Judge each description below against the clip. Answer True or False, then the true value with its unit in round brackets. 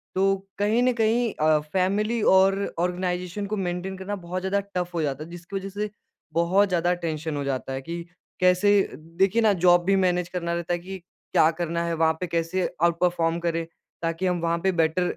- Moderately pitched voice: True (180 Hz)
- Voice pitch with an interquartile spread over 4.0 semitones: False (2.4 semitones)